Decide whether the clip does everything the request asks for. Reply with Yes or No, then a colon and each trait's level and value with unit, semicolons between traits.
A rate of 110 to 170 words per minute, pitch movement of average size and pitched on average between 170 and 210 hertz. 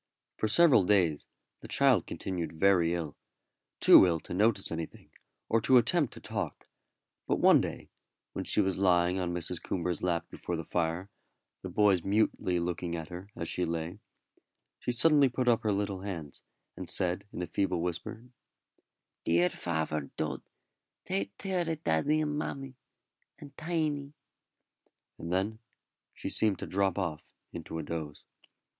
No: average, 155 wpm; average, 4.6 semitones; very low, 95 Hz